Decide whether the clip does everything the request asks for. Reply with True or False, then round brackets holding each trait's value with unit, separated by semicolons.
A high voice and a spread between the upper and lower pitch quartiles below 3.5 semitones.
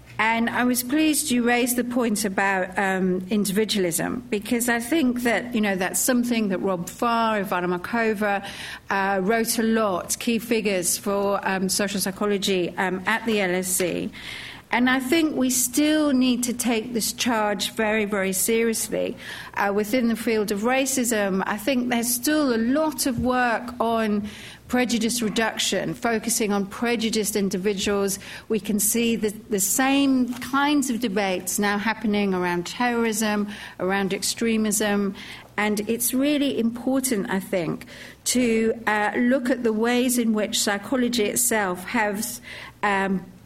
True (220 Hz; 3.1 semitones)